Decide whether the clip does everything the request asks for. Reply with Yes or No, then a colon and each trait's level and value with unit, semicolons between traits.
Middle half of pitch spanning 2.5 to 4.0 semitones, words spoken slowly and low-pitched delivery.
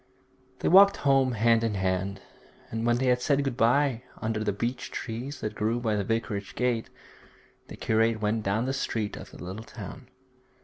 No: average, 2.8 semitones; average, 185 wpm; low, 115 Hz